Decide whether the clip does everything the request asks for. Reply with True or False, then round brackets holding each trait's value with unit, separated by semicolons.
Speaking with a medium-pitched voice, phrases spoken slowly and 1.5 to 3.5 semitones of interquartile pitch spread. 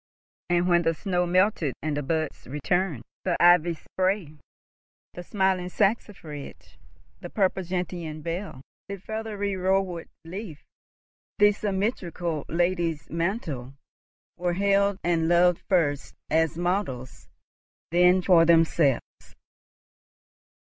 True (175 Hz; 105 wpm; 2.8 semitones)